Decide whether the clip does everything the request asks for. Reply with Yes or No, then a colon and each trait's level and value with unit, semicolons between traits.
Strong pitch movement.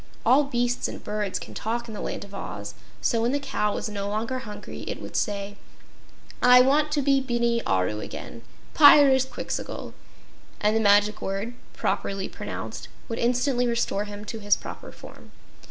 No: average, 3.7 semitones